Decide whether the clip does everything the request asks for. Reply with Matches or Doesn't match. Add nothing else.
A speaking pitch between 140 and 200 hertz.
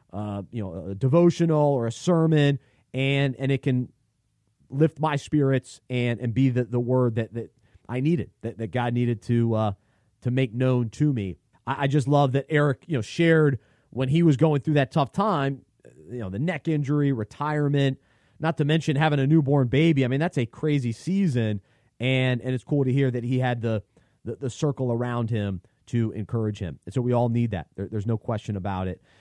Doesn't match